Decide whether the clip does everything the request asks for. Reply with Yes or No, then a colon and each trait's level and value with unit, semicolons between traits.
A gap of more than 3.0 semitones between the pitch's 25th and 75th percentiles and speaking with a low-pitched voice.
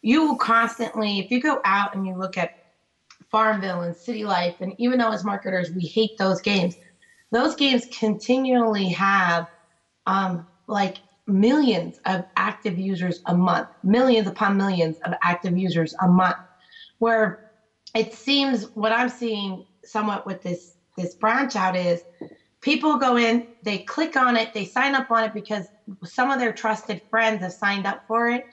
No: average, 3.8 semitones; high, 210 Hz